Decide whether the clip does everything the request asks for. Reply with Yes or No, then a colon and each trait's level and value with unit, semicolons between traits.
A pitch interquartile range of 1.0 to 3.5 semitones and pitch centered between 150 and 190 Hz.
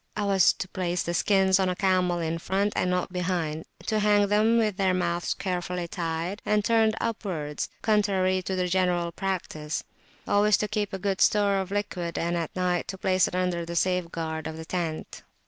Yes: average, 2.7 semitones; medium, 185 Hz